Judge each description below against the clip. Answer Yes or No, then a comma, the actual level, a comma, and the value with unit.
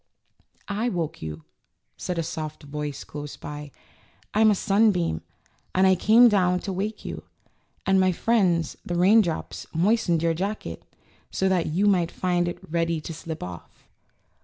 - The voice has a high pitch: No, medium, 175 Hz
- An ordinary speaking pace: Yes, average, 150 wpm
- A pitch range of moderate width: Yes, average, 3.6 semitones